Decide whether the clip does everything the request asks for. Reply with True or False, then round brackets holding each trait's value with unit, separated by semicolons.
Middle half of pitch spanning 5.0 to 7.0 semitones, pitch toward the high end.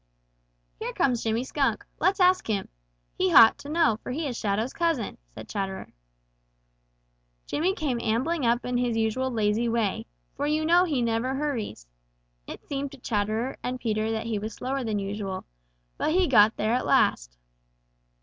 False (4.5 semitones; 235 Hz)